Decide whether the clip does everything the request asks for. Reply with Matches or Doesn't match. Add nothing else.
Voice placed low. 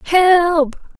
Doesn't match